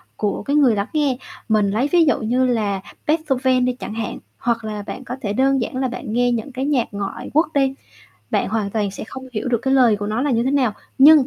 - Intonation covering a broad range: No, average, 3.7 semitones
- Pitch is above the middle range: Yes, high, 245 Hz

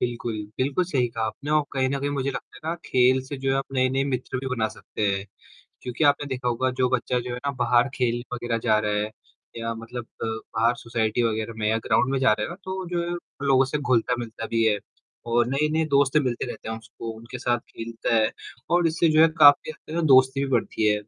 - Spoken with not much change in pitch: No, average, 3.3 semitones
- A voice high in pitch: No, low, 125 Hz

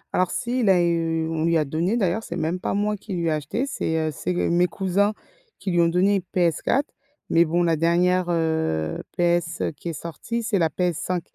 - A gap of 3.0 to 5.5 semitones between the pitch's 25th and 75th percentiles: No, narrow, 2.6 semitones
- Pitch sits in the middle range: Yes, medium, 175 Hz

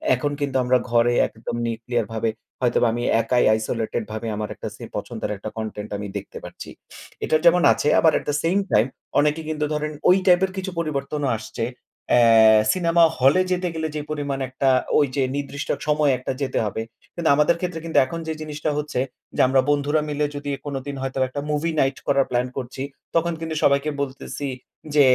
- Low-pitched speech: No, medium, 145 Hz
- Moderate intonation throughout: Yes, average, 3.7 semitones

